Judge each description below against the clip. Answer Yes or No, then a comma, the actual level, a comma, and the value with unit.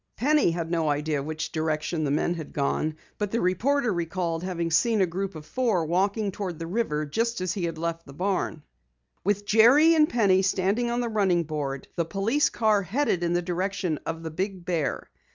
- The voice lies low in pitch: No, medium, 180 Hz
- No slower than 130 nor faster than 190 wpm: No, average, 200 wpm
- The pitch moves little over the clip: No, average, 4.3 semitones